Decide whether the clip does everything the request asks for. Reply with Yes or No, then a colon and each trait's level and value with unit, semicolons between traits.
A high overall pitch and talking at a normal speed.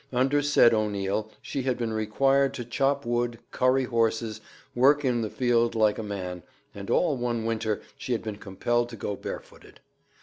No: low, 115 Hz; average, 175 wpm